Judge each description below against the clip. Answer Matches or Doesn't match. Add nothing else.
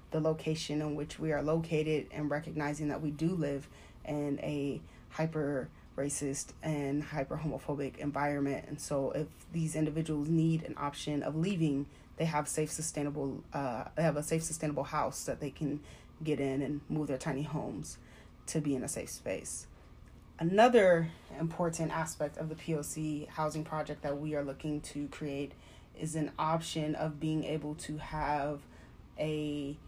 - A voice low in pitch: Doesn't match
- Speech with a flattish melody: Matches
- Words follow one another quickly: Doesn't match